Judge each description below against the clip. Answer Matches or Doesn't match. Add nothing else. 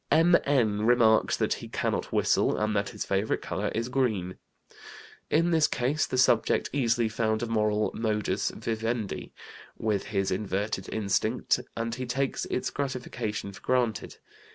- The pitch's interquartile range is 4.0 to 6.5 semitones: Doesn't match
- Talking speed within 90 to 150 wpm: Matches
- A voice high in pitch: Doesn't match